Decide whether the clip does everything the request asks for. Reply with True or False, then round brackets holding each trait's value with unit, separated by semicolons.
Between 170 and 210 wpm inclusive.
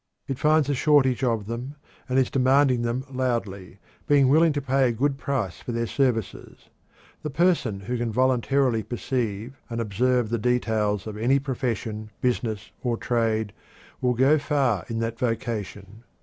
False (160 wpm)